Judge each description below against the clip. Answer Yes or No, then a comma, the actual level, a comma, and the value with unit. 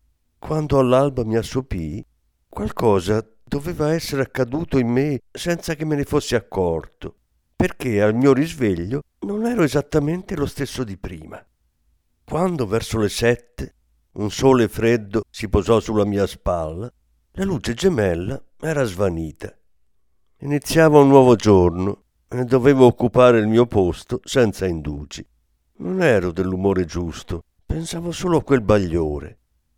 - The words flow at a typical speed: Yes, average, 130 wpm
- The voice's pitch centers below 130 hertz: Yes, low, 115 Hz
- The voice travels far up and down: Yes, wide, 8.1 semitones